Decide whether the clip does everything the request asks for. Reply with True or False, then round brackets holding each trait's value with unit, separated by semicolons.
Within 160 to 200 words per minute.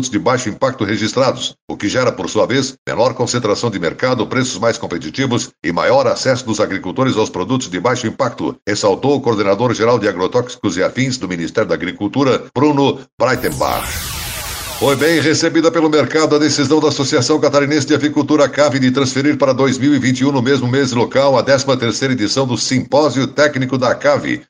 True (170 wpm)